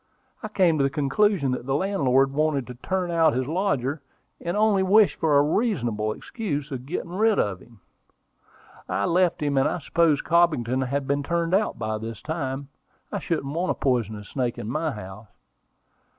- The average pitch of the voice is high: No, medium, 145 Hz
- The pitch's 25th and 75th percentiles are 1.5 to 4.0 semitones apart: No, average, 5.3 semitones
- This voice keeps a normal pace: Yes, average, 180 wpm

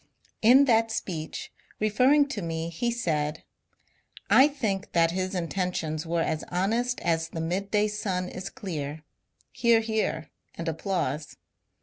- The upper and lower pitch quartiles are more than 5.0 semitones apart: Yes, wide, 5.4 semitones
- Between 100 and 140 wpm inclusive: Yes, slow, 135 wpm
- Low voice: No, medium, 185 Hz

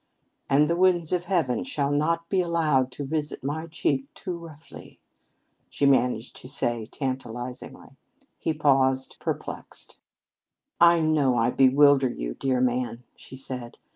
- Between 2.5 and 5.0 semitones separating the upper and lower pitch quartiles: Yes, average, 4.0 semitones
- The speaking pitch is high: No, medium, 140 Hz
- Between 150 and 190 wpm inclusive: No, average, 140 wpm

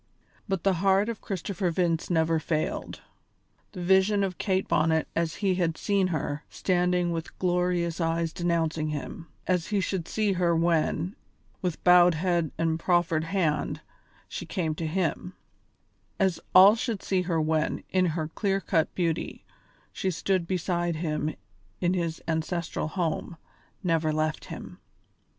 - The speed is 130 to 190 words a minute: Yes, average, 145 wpm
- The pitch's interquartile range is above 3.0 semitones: No, narrow, 2.5 semitones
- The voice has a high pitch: No, medium, 175 Hz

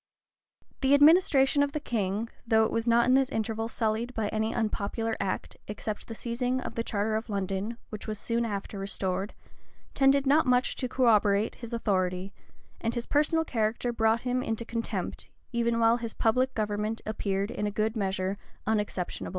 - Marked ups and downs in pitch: No, average, 2.8 semitones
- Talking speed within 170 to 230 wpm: Yes, average, 175 wpm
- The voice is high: Yes, high, 225 Hz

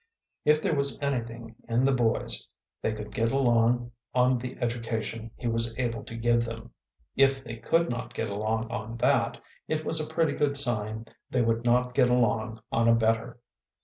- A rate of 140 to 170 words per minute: No, average, 180 wpm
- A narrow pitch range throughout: Yes, narrow, 2.1 semitones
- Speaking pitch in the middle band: No, low, 120 Hz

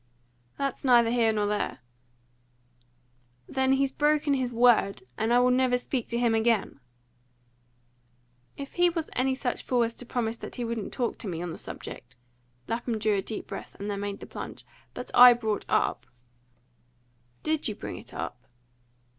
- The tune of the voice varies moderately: Yes, average, 3.7 semitones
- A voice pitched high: Yes, high, 235 Hz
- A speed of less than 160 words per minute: No, average, 175 wpm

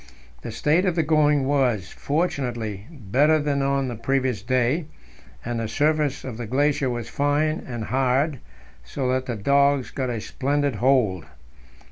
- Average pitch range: Yes, average, 3.4 semitones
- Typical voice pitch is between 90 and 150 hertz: Yes, low, 135 Hz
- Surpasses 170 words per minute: No, average, 155 wpm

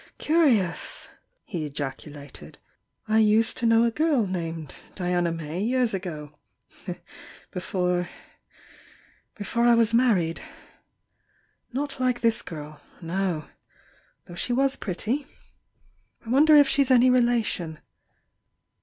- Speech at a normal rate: No, slow, 115 wpm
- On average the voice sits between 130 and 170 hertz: No, high, 210 Hz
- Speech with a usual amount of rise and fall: No, wide, 6.4 semitones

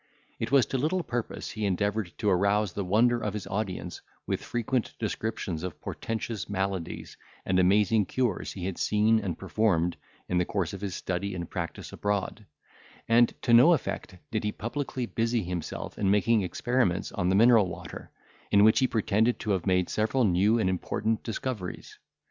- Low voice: Yes, low, 105 Hz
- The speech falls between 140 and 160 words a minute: No, average, 175 wpm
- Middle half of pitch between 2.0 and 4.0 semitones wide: Yes, average, 3.6 semitones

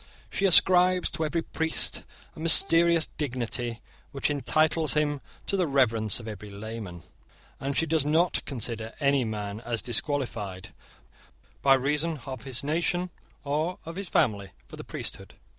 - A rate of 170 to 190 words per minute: No, average, 145 wpm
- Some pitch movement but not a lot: No, wide, 5.8 semitones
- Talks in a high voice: No, medium, 140 Hz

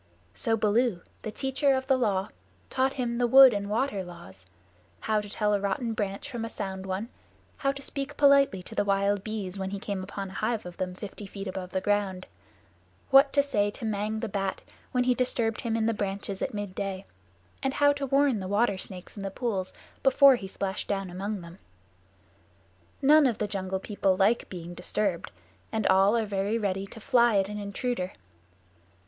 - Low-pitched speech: No, high, 205 Hz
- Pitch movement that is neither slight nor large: Yes, average, 3.8 semitones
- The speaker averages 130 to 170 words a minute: No, average, 195 wpm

